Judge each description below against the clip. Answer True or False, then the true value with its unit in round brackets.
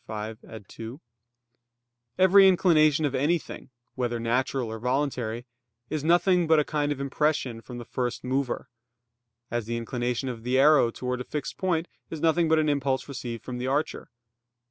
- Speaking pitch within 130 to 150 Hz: True (135 Hz)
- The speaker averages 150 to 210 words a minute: True (165 wpm)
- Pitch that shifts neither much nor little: True (4.2 semitones)